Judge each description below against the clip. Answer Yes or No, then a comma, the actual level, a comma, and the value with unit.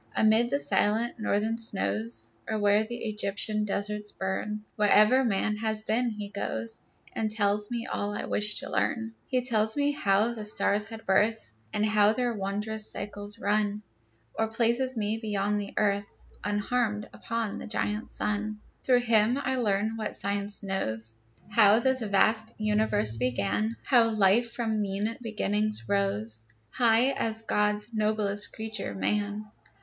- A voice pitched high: Yes, high, 210 Hz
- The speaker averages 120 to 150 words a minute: Yes, average, 145 wpm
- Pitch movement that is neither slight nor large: No, narrow, 1.7 semitones